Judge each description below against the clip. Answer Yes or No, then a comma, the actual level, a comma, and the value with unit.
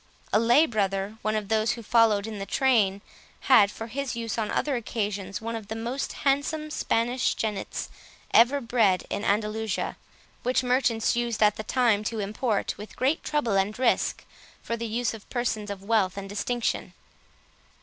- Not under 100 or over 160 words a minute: No, average, 170 wpm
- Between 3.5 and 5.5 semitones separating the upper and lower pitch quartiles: No, average, 2.7 semitones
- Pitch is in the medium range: No, high, 225 Hz